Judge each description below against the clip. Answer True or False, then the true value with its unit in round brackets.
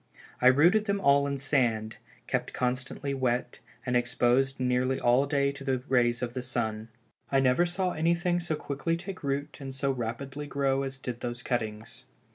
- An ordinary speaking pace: True (175 wpm)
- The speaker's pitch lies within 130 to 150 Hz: True (135 Hz)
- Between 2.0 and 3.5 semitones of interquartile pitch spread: True (2.5 semitones)